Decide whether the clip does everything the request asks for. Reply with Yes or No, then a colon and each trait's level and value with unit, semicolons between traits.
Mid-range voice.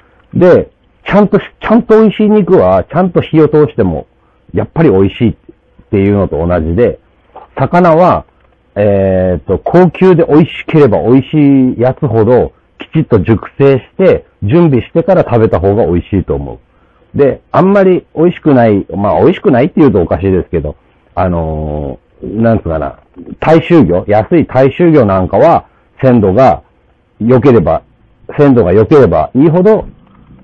No: low, 120 Hz